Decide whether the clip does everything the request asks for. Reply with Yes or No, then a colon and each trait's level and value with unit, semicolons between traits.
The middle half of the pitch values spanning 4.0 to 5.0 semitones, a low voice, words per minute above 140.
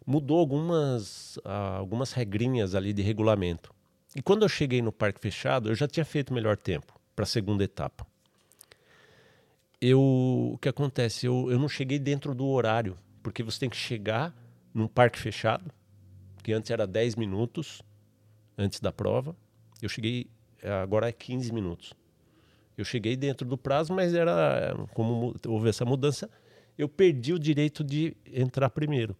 Yes: average, 4.5 semitones; low, 120 Hz; average, 155 wpm